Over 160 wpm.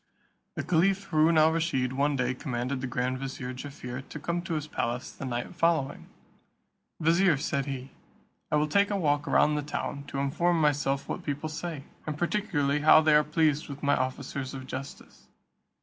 Yes: average, 180 wpm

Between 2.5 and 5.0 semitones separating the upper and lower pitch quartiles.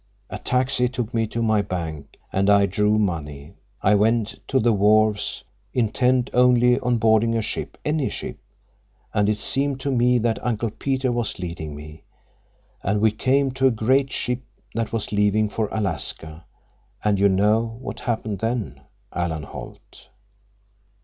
Yes: average, 3.5 semitones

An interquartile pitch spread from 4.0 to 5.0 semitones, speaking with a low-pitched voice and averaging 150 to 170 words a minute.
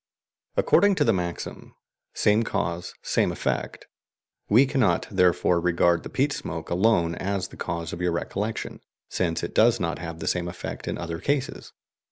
Yes: average, 4.7 semitones; very low, 90 Hz; average, 165 wpm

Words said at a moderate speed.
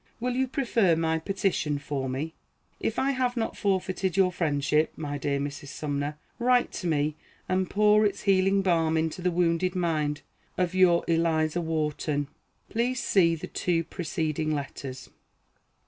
Yes: average, 155 wpm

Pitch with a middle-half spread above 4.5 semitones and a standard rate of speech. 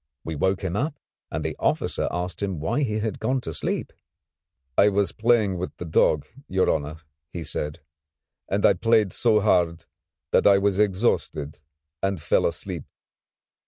No: average, 3.9 semitones; average, 160 wpm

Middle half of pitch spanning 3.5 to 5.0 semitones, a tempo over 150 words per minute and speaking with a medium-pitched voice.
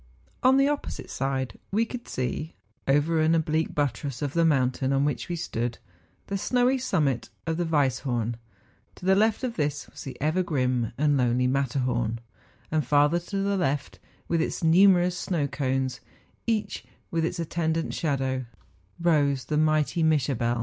Yes: average, 4.6 semitones; average, 165 wpm; medium, 150 Hz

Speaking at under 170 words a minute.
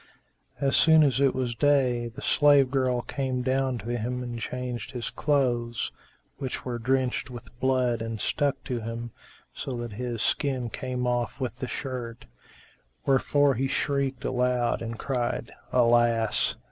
Yes: average, 150 wpm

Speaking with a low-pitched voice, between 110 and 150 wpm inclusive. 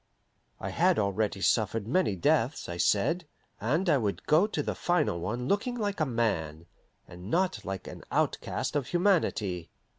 No: low, 120 Hz; average, 160 wpm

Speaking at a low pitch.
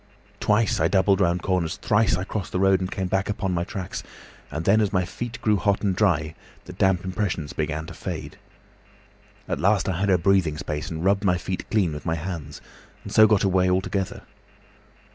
Yes: very low, 95 Hz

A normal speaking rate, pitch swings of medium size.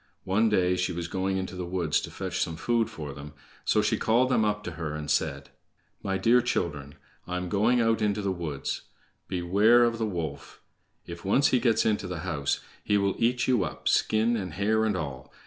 No: fast, 215 wpm; average, 4.5 semitones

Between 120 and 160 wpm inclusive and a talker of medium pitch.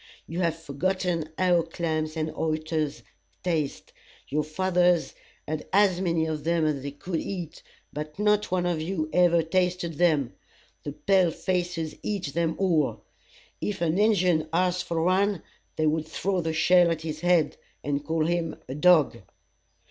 Yes: average, 155 wpm; medium, 165 Hz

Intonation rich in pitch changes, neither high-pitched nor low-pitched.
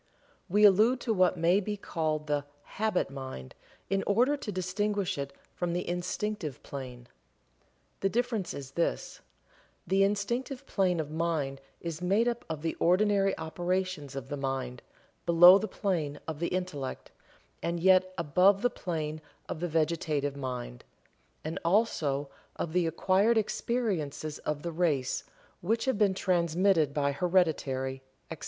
No: average, 4.9 semitones; medium, 175 Hz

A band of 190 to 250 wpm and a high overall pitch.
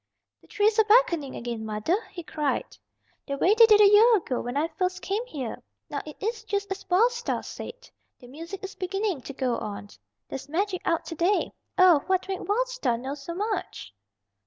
Yes: average, 200 wpm; very high, 365 Hz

